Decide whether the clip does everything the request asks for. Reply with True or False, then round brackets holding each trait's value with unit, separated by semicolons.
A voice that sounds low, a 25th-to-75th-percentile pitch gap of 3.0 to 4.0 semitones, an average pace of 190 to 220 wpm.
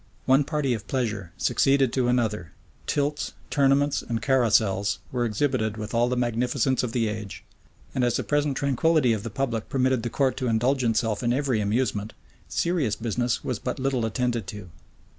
False (120 Hz; 3.3 semitones; 175 wpm)